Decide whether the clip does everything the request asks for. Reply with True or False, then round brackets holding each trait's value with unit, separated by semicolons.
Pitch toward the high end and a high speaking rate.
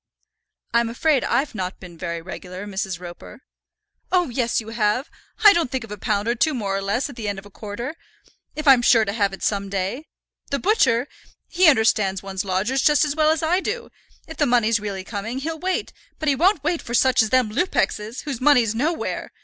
True (235 Hz; 215 wpm)